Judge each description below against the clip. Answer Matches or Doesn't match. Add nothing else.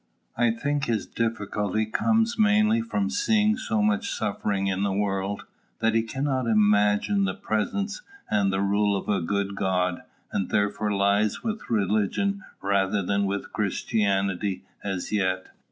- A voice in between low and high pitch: Doesn't match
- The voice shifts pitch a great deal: Matches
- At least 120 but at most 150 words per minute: Matches